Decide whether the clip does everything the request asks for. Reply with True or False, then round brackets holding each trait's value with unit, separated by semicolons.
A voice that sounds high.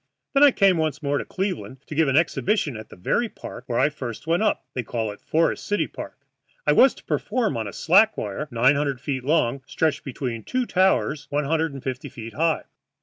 False (145 Hz)